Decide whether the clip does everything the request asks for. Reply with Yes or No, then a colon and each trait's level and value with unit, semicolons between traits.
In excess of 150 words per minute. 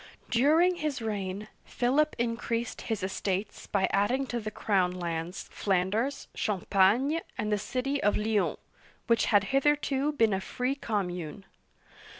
No: slow, 135 wpm